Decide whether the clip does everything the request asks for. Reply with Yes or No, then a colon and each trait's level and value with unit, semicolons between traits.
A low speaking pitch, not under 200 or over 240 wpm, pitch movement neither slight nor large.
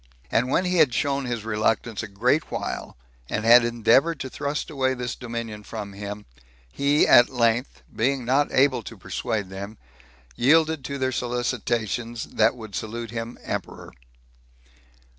No: low, 120 Hz; average, 150 wpm; average, 3.1 semitones